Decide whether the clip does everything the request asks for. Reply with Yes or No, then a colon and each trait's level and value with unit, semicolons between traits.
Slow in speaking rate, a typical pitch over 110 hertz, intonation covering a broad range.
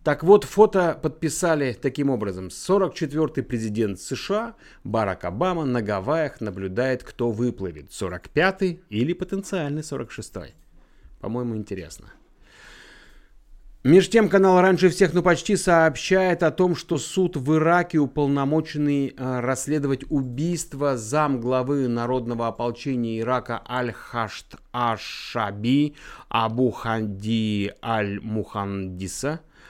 Yes: slow, 100 wpm; low, 135 Hz; wide, 6.2 semitones